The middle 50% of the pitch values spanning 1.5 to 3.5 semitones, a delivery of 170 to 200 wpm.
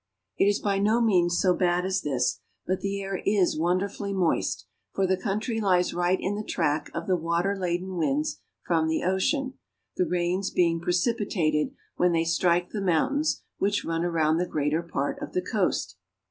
Yes: average, 2.8 semitones; average, 190 wpm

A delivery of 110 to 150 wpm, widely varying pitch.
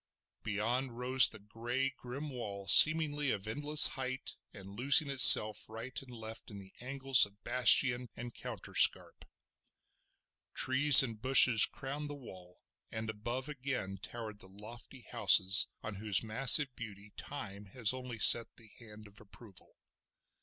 No: average, 140 wpm; average, 3.9 semitones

